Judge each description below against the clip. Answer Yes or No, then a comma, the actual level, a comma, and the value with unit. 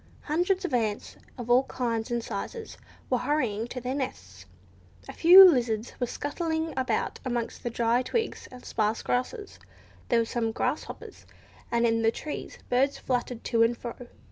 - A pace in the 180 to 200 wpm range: No, average, 165 wpm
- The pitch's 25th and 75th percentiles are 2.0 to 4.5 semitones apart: Yes, average, 3.8 semitones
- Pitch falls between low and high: No, high, 245 Hz